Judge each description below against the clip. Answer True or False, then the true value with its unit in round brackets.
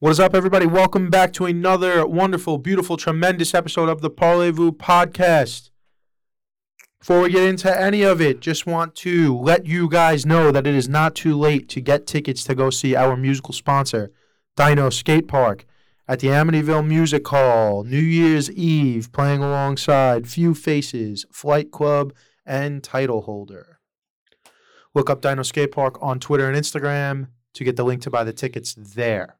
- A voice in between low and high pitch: True (145 Hz)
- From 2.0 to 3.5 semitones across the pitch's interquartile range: False (4.1 semitones)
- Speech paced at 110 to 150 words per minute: False (165 wpm)